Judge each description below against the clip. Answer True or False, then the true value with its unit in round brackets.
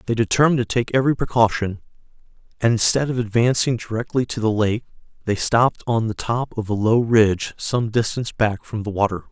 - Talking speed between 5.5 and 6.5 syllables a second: True (5.9 syllables/s)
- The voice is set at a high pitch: False (115 Hz)